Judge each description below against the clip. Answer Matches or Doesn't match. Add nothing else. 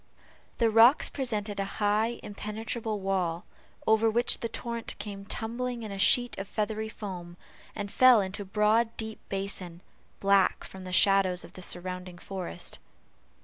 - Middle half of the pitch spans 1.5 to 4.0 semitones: Matches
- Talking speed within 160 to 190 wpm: Doesn't match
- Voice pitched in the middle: Doesn't match